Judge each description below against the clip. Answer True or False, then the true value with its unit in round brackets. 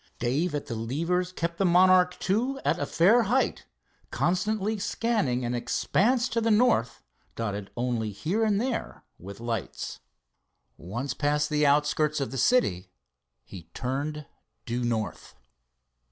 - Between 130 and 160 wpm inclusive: True (140 wpm)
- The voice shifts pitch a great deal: True (8.8 semitones)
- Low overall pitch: False (150 Hz)